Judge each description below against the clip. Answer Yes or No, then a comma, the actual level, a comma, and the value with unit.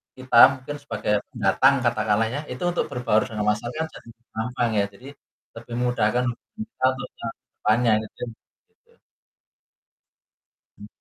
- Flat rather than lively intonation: No, average, 3.6 semitones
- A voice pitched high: No, low, 125 Hz